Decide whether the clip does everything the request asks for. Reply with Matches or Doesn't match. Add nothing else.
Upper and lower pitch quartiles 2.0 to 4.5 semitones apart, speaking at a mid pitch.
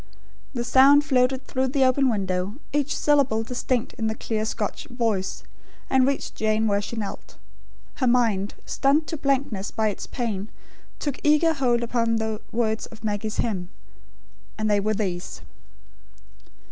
Doesn't match